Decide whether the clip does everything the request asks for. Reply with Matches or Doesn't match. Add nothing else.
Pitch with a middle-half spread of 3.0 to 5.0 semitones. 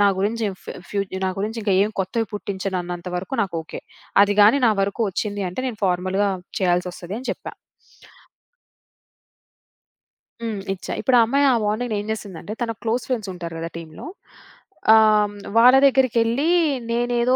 Matches